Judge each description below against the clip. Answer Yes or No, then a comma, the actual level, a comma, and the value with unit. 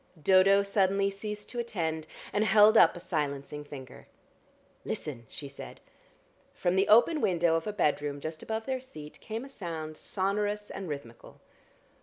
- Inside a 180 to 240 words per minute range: No, average, 155 wpm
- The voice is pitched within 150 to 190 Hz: Yes, medium, 185 Hz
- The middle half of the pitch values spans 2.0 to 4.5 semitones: No, average, 5.3 semitones